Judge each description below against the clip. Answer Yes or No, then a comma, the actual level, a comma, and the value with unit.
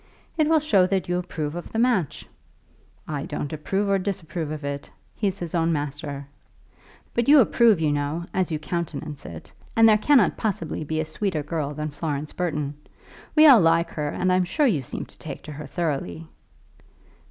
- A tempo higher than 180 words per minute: Yes, average, 190 wpm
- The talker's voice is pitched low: No, medium, 165 Hz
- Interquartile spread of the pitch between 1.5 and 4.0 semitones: No, average, 4.8 semitones